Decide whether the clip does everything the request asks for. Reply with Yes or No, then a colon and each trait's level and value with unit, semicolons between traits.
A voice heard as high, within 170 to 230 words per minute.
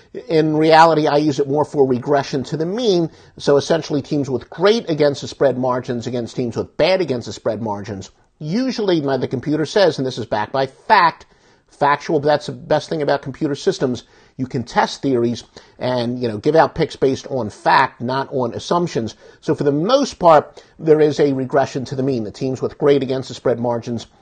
No: medium, 140 Hz; fast, 205 wpm